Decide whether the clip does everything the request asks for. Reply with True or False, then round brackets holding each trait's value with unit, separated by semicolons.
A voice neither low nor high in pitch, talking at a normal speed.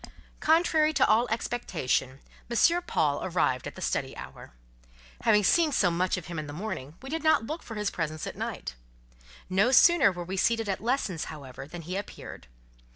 False (200 Hz; 185 wpm)